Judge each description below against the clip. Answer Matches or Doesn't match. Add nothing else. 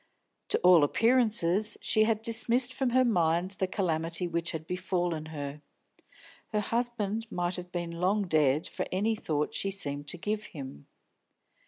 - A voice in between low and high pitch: Matches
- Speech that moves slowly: Doesn't match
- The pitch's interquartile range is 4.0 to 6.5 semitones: Matches